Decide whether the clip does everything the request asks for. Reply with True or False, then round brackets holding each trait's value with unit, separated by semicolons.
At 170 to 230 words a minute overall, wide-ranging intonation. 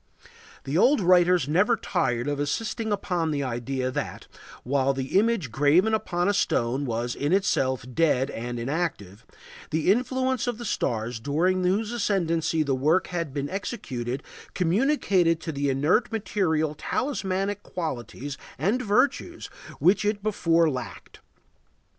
False (140 wpm; 6.8 semitones)